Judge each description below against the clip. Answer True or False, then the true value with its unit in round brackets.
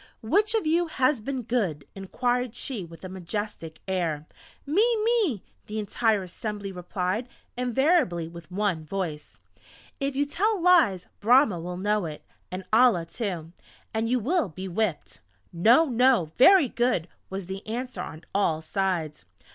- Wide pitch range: True (6.2 semitones)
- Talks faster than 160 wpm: False (150 wpm)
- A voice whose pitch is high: True (210 Hz)